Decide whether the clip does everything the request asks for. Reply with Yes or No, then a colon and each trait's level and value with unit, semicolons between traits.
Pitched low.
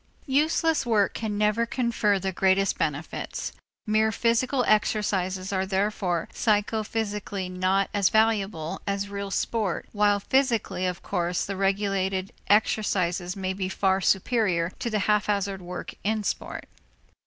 No: high, 200 Hz